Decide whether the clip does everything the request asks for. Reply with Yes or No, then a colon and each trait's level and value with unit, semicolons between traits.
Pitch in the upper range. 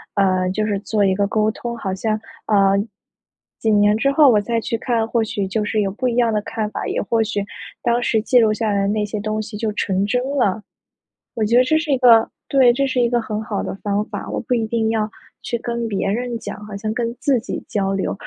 Yes: high, 220 Hz